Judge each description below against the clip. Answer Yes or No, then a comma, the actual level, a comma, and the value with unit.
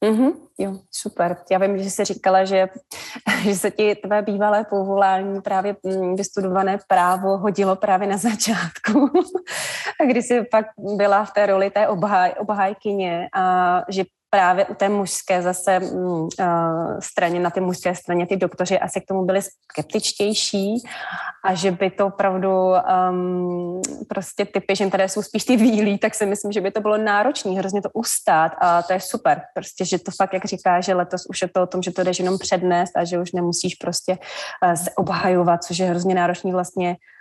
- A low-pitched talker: No, high, 195 Hz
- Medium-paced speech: No, fast, 180 wpm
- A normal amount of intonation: No, narrow, 2.3 semitones